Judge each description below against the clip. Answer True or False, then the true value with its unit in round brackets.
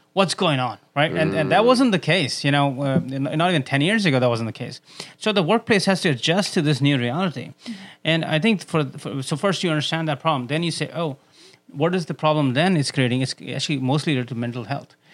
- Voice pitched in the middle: True (155 Hz)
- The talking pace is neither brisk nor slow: False (240 wpm)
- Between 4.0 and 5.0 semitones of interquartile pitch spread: True (4.3 semitones)